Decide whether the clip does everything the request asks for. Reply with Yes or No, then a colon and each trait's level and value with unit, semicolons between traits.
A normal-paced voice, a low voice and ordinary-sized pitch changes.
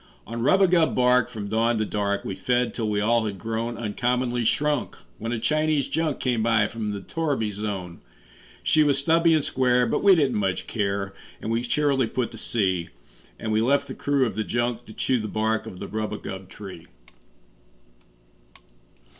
Yes: average, 180 wpm; low, 115 Hz; average, 3.8 semitones